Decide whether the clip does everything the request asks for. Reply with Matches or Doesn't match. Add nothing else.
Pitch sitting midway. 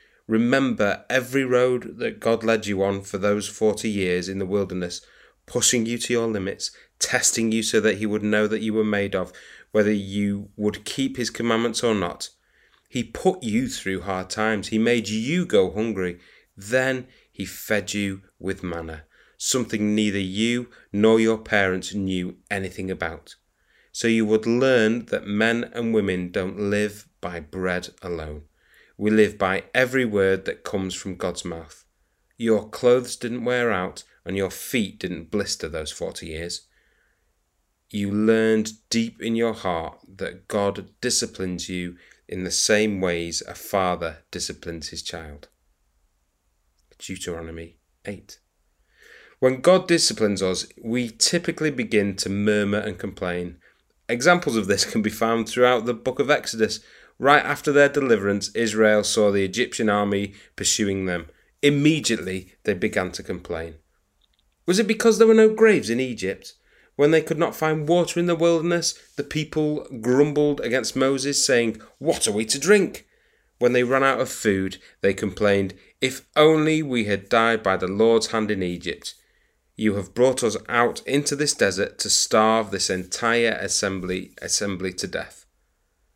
Doesn't match